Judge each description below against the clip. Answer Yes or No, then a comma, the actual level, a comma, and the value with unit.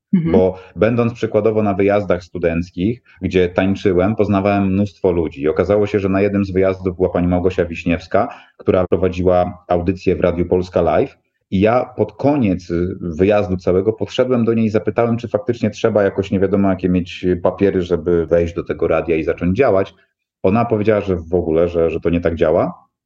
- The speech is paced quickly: Yes, fast, 175 wpm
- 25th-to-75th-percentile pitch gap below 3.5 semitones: Yes, average, 2.7 semitones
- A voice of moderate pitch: No, very low, 95 Hz